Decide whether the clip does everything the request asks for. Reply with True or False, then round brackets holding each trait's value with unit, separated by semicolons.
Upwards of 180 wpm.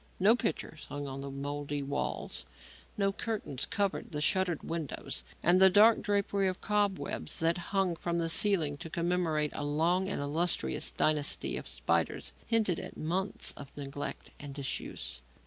False (155 wpm)